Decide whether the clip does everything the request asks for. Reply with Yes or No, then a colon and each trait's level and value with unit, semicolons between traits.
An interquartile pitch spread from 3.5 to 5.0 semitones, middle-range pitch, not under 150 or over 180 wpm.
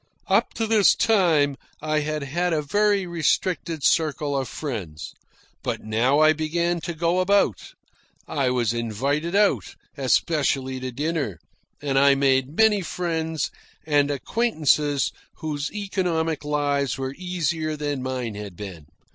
No: average, 4.1 semitones; medium, 150 Hz; slow, 135 wpm